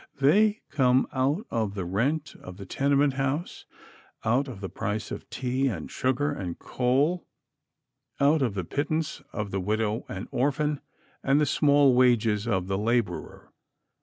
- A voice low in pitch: Yes, low, 130 Hz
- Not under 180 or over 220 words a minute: No, average, 155 wpm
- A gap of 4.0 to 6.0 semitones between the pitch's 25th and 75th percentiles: Yes, wide, 5.4 semitones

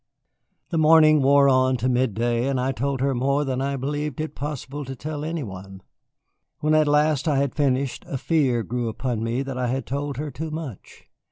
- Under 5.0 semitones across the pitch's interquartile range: Yes, average, 2.7 semitones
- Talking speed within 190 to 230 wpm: Yes, average, 200 wpm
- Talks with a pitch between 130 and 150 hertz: Yes, low, 135 Hz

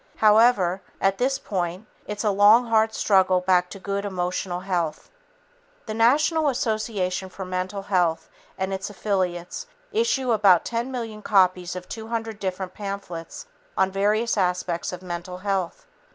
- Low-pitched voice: No, high, 195 Hz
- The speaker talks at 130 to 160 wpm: Yes, average, 140 wpm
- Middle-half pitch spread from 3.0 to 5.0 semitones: Yes, average, 3.3 semitones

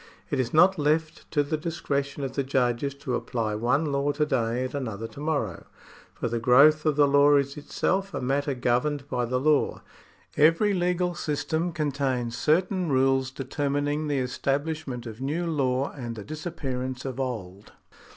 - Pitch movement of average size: Yes, average, 3.2 semitones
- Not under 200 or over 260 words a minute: No, average, 170 wpm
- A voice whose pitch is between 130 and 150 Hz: Yes, medium, 140 Hz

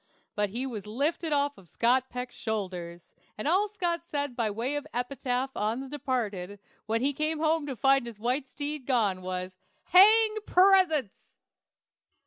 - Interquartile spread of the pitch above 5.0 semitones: Yes, wide, 5.6 semitones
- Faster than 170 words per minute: No, average, 155 wpm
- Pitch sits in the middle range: No, very high, 260 Hz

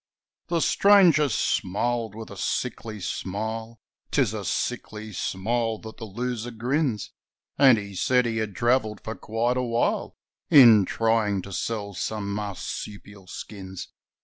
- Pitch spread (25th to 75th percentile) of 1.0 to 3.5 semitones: Yes, average, 2.9 semitones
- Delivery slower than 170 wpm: Yes, slow, 135 wpm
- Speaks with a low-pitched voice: Yes, low, 110 Hz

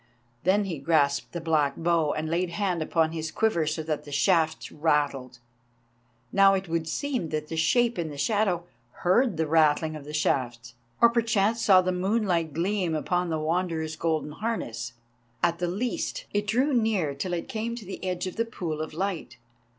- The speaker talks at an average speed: Yes, average, 180 wpm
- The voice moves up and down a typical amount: Yes, average, 4.2 semitones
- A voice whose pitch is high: No, medium, 170 Hz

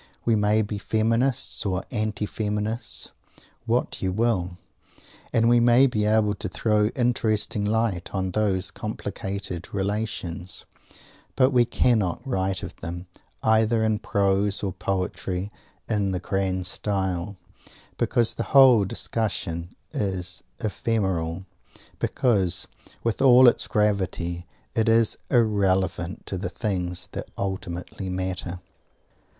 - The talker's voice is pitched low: Yes, low, 100 Hz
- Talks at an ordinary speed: No, slow, 120 wpm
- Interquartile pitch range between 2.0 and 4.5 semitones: Yes, average, 3.1 semitones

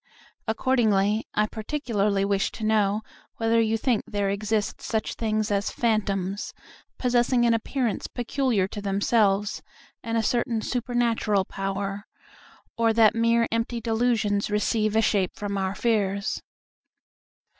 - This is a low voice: No, high, 215 Hz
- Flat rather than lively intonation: Yes, narrow, 2.3 semitones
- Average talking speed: No, slow, 125 wpm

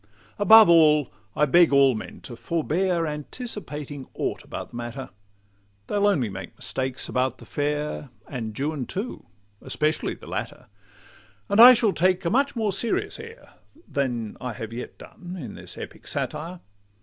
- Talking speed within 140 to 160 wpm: Yes, average, 155 wpm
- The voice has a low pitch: No, medium, 150 Hz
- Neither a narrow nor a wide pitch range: No, wide, 6.7 semitones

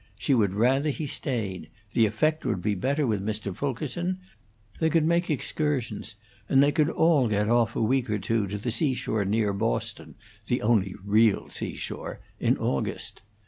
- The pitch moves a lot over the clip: Yes, wide, 5.7 semitones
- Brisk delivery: No, average, 170 wpm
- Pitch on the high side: No, low, 115 Hz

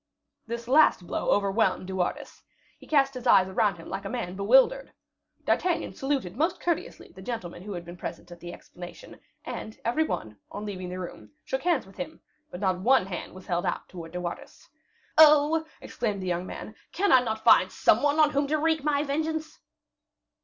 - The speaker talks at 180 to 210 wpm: Yes, average, 195 wpm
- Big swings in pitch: Yes, wide, 8.1 semitones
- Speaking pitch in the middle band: No, high, 220 Hz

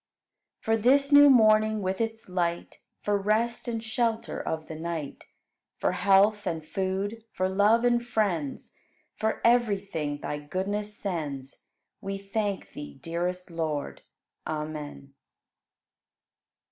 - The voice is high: Yes, high, 195 Hz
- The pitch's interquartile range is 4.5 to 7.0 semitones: Yes, average, 5.1 semitones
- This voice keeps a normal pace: No, slow, 120 wpm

